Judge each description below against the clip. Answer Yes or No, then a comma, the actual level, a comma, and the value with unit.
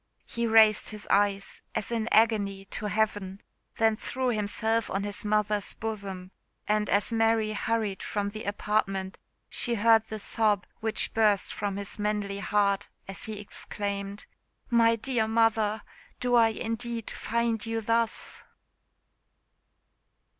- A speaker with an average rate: No, slow, 130 wpm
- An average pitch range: No, narrow, 1.9 semitones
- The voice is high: Yes, high, 215 Hz